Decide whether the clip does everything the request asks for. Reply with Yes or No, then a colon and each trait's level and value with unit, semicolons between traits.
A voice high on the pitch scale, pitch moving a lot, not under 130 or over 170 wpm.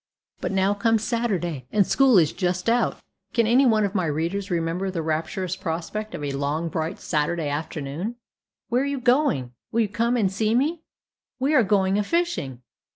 No: high, 195 Hz; wide, 6.1 semitones; average, 185 wpm